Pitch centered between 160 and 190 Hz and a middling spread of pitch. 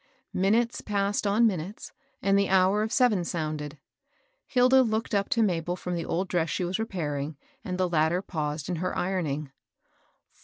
Yes: medium, 185 Hz; average, 4.2 semitones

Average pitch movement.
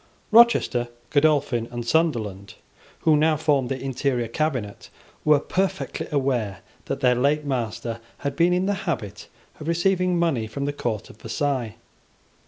Yes: average, 5.0 semitones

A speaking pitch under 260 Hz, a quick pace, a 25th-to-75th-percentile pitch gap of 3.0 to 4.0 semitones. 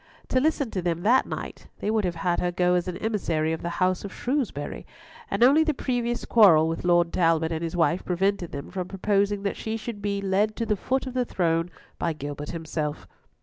No: medium, 185 Hz; fast, 220 wpm; average, 4.7 semitones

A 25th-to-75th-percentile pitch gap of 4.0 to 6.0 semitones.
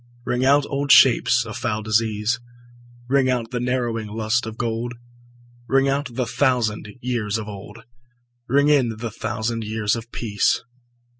No: narrow, 2.6 semitones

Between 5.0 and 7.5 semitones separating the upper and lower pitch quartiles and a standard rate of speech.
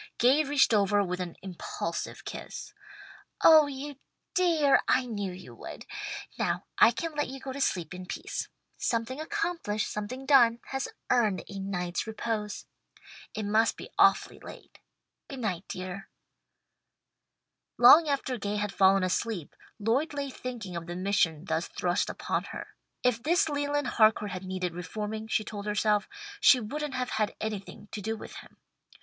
Yes: wide, 5.6 semitones; average, 155 wpm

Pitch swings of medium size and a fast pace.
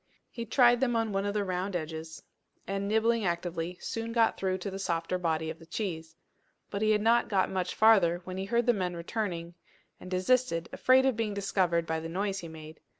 Yes: average, 4.6 semitones; fast, 210 wpm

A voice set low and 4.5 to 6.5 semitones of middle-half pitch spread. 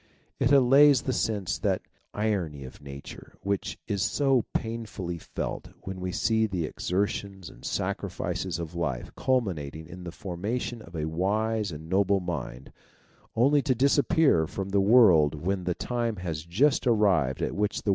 Yes: very low, 95 Hz; average, 5.0 semitones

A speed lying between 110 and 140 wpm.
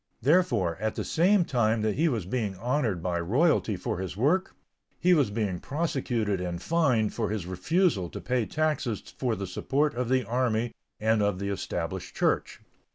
No: average, 175 wpm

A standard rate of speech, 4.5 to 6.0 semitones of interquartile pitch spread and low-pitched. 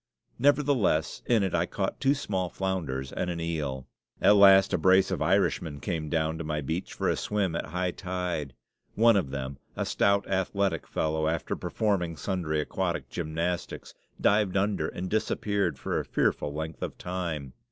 No: average, 170 wpm; average, 3.8 semitones; very low, 90 Hz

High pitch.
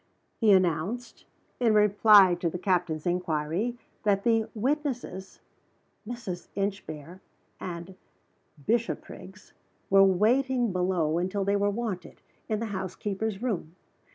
Yes: high, 195 Hz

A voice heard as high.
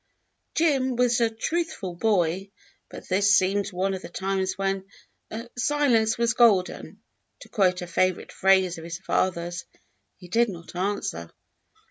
Yes: high, 195 Hz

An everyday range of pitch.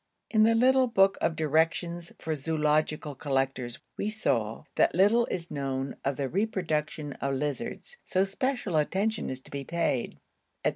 No: wide, 6.1 semitones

